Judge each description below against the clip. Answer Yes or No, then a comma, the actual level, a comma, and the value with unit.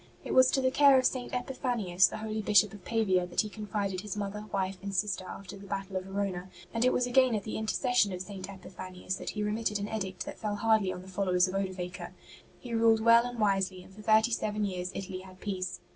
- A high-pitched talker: Yes, high, 205 Hz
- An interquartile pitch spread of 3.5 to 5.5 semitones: No, average, 2.9 semitones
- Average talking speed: No, fast, 235 wpm